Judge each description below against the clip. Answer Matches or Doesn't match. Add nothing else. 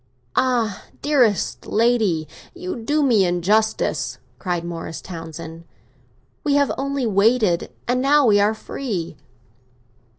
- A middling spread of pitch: Doesn't match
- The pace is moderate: Doesn't match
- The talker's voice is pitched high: Matches